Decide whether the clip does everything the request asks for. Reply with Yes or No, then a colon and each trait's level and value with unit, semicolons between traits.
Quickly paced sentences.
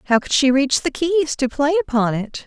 Yes: fast, 245 wpm